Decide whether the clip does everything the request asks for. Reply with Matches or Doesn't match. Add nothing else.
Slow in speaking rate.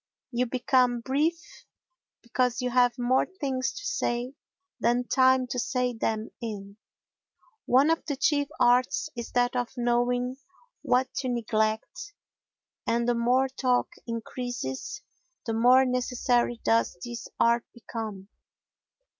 Matches